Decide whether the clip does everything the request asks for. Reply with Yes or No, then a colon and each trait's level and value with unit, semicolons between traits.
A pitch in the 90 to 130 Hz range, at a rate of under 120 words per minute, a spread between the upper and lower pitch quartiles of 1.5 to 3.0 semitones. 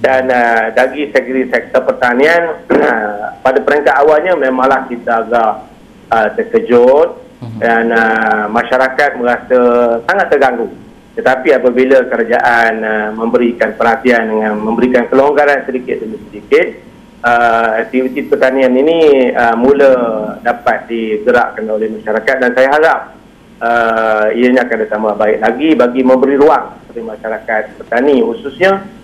No: low, 120 Hz; average, 125 wpm; narrow, 2.6 semitones